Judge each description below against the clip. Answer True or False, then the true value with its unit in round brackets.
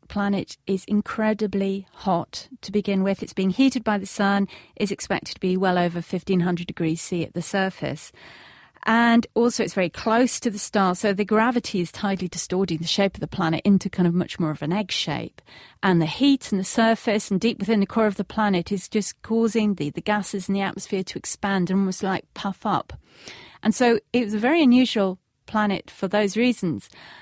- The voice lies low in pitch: False (200 Hz)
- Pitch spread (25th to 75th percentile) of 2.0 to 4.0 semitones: True (3.1 semitones)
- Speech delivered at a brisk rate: True (210 wpm)